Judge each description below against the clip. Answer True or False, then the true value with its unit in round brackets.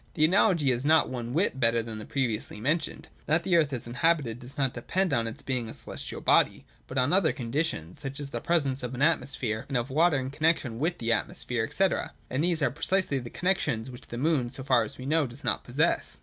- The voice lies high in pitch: False (135 Hz)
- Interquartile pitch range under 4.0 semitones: False (4.9 semitones)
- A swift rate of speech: True (230 wpm)